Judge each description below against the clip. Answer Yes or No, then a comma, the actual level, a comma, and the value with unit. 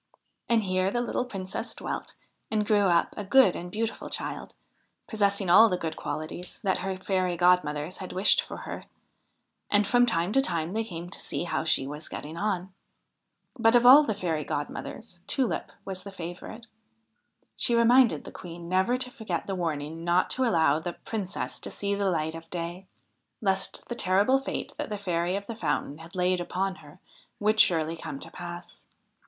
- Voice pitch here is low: No, medium, 185 Hz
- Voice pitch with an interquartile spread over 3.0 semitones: Yes, average, 3.9 semitones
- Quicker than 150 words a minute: Yes, average, 185 wpm